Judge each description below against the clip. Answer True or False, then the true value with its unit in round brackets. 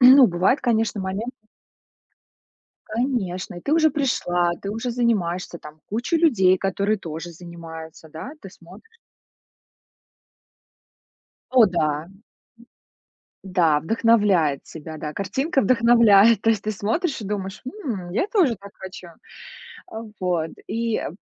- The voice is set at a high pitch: True (200 Hz)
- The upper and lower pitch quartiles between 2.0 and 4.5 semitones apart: False (5.0 semitones)